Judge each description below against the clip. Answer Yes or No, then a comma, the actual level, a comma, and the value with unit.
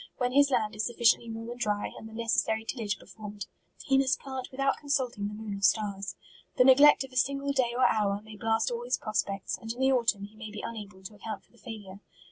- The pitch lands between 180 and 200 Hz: No, high, 225 Hz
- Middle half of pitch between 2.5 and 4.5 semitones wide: Yes, average, 3.5 semitones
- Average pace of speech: No, fast, 250 wpm